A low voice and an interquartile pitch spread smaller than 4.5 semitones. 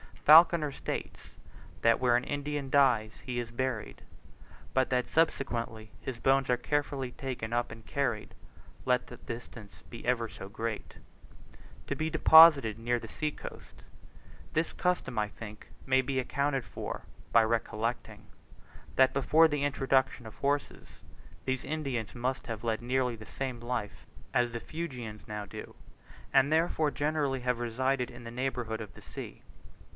Yes: low, 125 Hz; average, 3.3 semitones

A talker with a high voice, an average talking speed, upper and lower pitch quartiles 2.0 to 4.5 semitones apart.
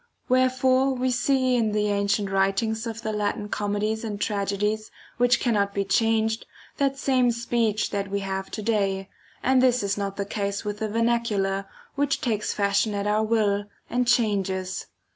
Yes: high, 215 Hz; average, 170 wpm; average, 2.9 semitones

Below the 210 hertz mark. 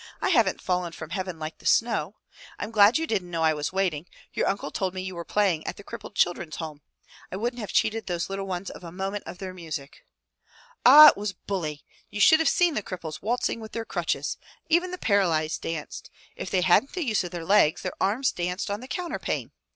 Yes: high, 190 Hz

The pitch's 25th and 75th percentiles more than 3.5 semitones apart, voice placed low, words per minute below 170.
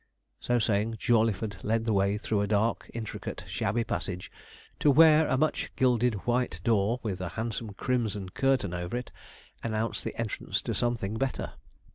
No: average, 3.1 semitones; low, 115 Hz; average, 160 wpm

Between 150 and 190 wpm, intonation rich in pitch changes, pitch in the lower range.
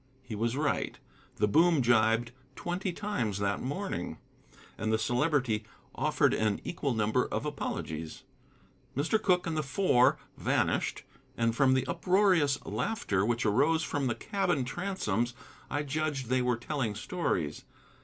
No: average, 140 wpm; wide, 6.4 semitones; low, 130 Hz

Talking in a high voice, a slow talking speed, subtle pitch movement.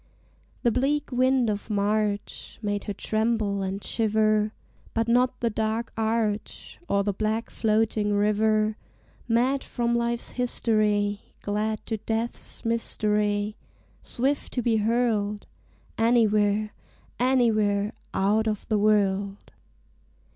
Yes: high, 215 Hz; slow, 110 wpm; narrow, 2.0 semitones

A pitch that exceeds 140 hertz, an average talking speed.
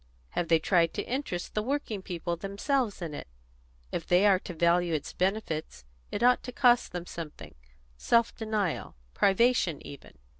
Yes: medium, 185 Hz; average, 160 wpm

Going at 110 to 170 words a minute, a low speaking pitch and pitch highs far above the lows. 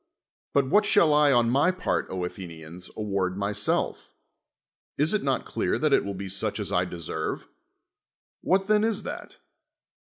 Yes: average, 160 wpm; low, 115 Hz; wide, 9.0 semitones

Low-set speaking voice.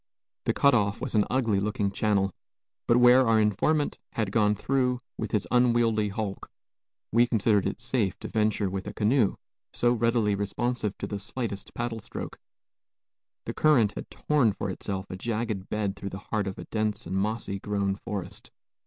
Yes: low, 110 Hz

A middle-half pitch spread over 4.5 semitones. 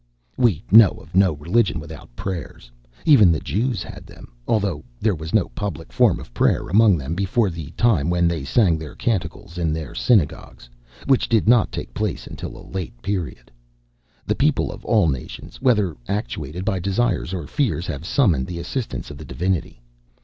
Yes: average, 5.0 semitones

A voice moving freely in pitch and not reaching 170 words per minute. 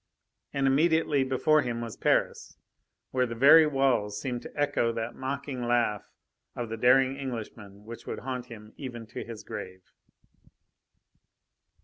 No: average, 3.0 semitones; average, 140 wpm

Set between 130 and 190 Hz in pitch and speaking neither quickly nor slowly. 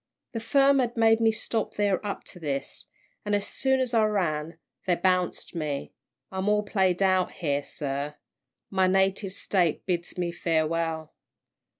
Yes: medium, 185 Hz; average, 160 wpm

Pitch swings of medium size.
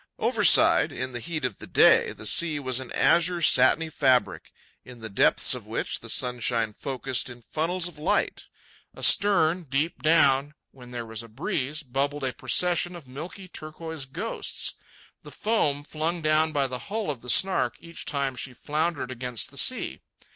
Yes: average, 4.4 semitones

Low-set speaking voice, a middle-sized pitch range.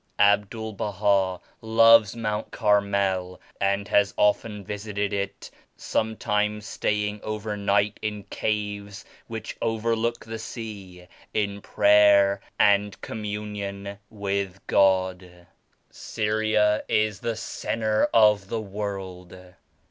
No: low, 105 Hz; narrow, 1.4 semitones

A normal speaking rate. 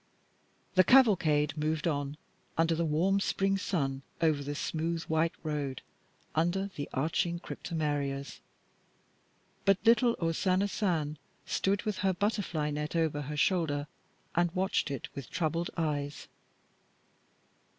No: slow, 125 wpm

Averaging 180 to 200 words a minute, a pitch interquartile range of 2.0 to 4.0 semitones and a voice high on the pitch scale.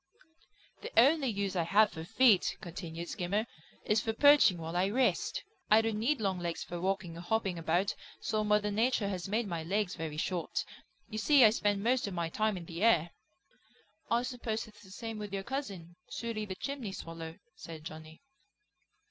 No: average, 185 wpm; average, 4.4 semitones; high, 200 Hz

